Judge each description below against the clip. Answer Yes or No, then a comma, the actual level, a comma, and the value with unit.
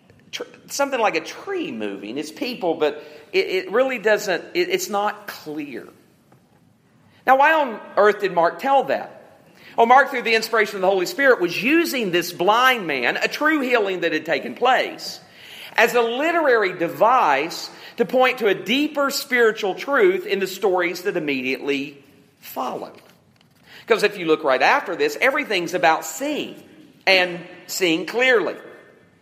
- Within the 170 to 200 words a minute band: No, average, 155 wpm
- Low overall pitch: No, high, 215 Hz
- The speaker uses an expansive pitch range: Yes, wide, 7.4 semitones